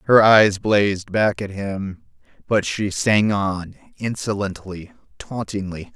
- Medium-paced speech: No, slow, 120 wpm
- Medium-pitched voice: No, low, 105 Hz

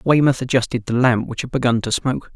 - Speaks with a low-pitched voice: Yes, low, 125 Hz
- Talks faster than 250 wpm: No, fast, 230 wpm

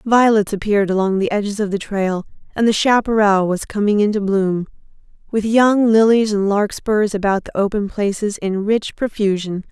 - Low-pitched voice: No, high, 205 Hz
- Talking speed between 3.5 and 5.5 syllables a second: Yes, 5.0 syllables/s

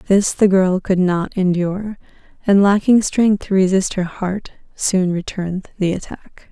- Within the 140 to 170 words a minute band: Yes, average, 165 wpm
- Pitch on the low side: No, high, 190 Hz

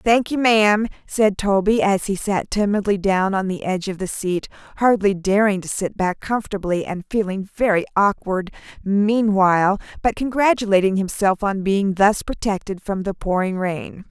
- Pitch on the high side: Yes, high, 200 Hz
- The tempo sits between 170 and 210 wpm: No, average, 160 wpm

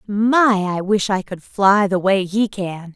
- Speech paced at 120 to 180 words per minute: No, fast, 205 wpm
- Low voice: No, high, 200 Hz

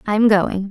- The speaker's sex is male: No, female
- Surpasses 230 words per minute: Yes, fast, 255 wpm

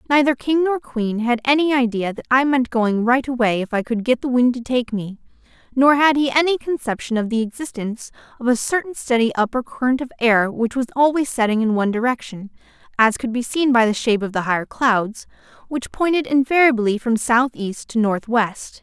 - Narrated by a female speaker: Yes, female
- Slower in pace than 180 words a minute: No, average, 200 wpm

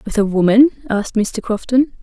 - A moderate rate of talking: Yes, average, 180 wpm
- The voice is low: No, high, 225 Hz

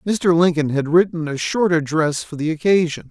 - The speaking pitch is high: No, medium, 165 Hz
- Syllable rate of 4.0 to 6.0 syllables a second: Yes, 5.1 syllables/s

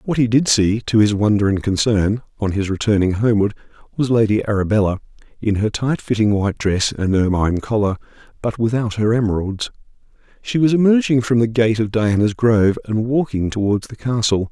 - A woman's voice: No, male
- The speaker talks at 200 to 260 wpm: No, average, 180 wpm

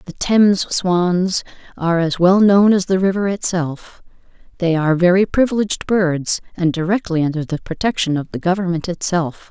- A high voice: No, medium, 180 Hz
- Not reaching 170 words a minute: Yes, average, 160 wpm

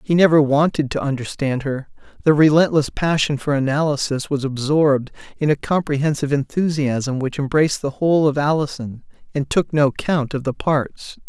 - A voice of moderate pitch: Yes, medium, 145 Hz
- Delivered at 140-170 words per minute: Yes, average, 160 wpm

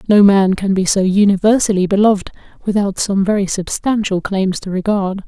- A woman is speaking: Yes, female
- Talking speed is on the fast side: No, average, 160 wpm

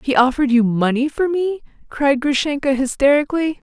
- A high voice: Yes, very high, 275 Hz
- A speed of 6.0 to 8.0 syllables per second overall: No, 5.5 syllables/s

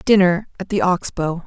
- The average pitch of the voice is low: No, medium, 185 Hz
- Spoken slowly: No, fast, 205 wpm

